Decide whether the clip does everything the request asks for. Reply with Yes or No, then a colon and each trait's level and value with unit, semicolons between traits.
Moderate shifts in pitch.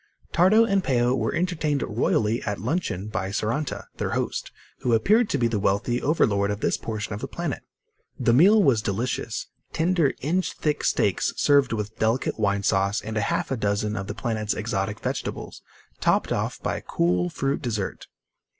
No: wide, 5.8 semitones